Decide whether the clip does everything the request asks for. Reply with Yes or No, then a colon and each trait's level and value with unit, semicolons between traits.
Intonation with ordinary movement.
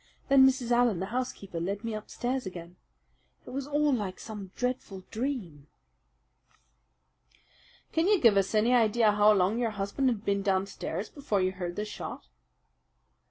Yes: average, 4.3 semitones